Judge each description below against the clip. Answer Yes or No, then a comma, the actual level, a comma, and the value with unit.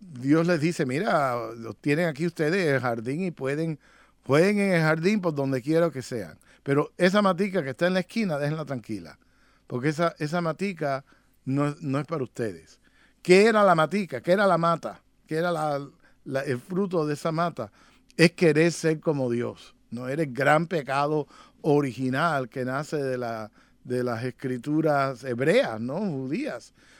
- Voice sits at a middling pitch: Yes, medium, 150 Hz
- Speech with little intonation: No, average, 4.8 semitones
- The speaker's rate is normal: Yes, average, 170 wpm